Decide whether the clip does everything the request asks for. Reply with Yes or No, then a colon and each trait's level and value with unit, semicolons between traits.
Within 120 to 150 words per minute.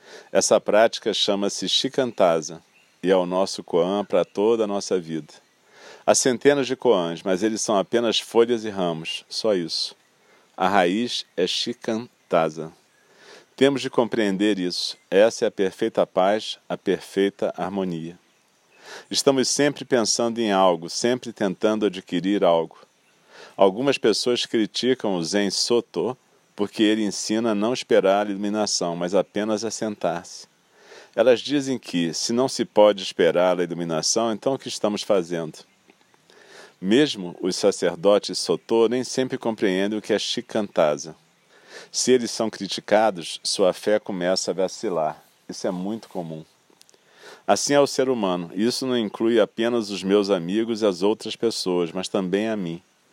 Yes: average, 145 wpm